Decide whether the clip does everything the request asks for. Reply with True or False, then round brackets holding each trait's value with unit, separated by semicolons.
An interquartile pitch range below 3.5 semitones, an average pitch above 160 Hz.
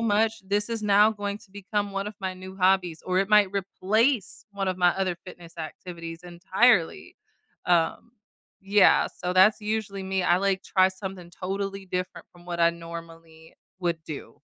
True (2.5 semitones; 190 Hz)